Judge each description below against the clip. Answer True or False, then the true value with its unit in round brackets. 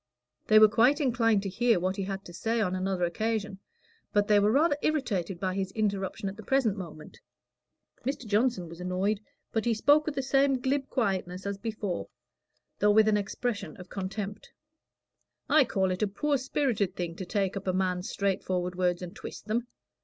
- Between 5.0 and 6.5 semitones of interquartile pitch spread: False (3.7 semitones)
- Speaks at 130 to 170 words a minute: False (195 wpm)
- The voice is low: False (205 Hz)